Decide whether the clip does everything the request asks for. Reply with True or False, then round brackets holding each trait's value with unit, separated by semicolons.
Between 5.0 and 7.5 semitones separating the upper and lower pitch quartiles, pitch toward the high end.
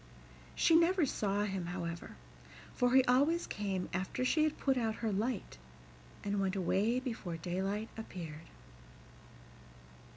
True (5.3 semitones; 210 Hz)